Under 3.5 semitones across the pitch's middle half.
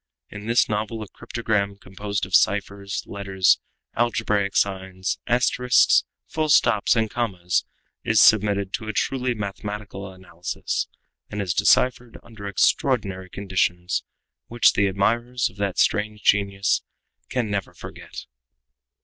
Yes: average, 2.8 semitones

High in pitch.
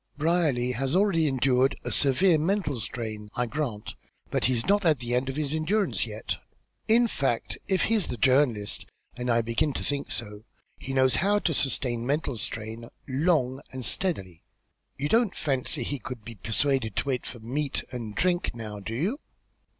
No: low, 130 Hz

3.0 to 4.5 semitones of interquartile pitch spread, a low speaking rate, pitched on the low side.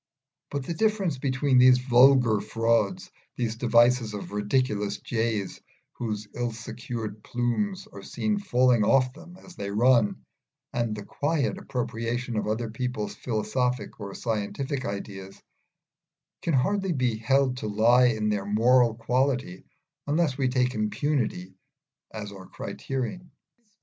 Yes: average, 3.6 semitones; slow, 130 wpm; low, 120 Hz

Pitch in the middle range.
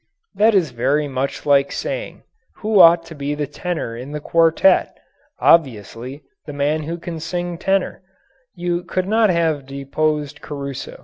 Yes: medium, 155 Hz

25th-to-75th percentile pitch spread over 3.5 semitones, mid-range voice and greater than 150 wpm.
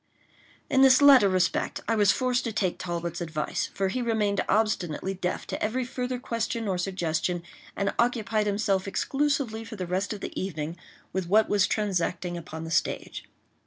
No: average, 4.2 semitones; high, 200 Hz; average, 170 wpm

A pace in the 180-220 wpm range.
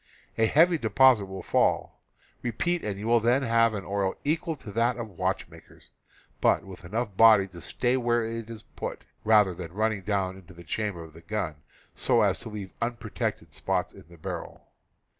Yes: average, 185 wpm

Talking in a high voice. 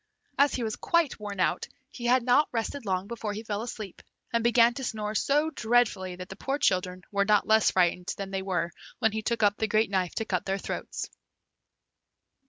Yes: high, 215 Hz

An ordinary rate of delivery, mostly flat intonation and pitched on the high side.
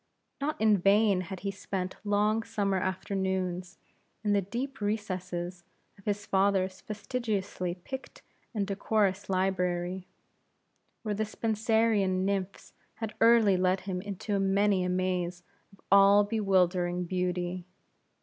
No: slow, 120 wpm; narrow, 2.1 semitones; high, 195 Hz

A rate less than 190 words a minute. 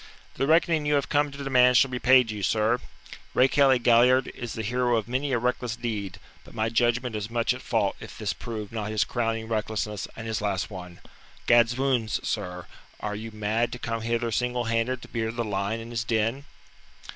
No: average, 200 wpm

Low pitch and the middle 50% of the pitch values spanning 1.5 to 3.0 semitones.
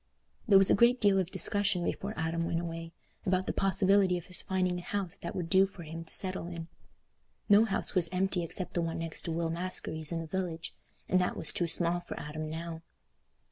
No: medium, 175 Hz; narrow, 2.4 semitones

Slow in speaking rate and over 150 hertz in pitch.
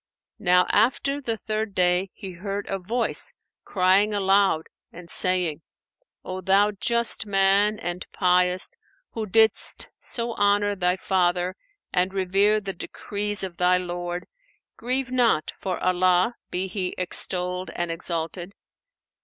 Yes: slow, 130 wpm; high, 190 Hz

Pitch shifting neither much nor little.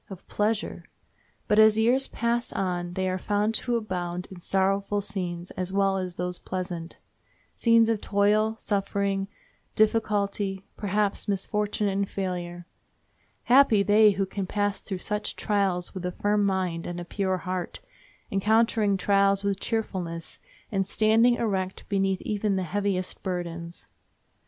No: narrow, 2.3 semitones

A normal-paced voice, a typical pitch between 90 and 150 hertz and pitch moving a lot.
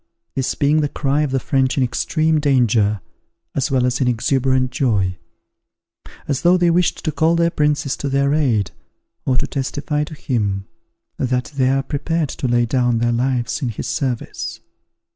No: average, 175 wpm; low, 135 Hz; average, 3.2 semitones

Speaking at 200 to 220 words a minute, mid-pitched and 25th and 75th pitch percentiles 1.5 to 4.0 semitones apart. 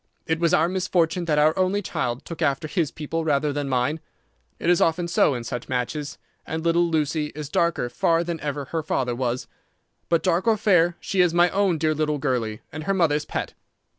Yes: fast, 205 wpm; medium, 160 Hz; average, 3.0 semitones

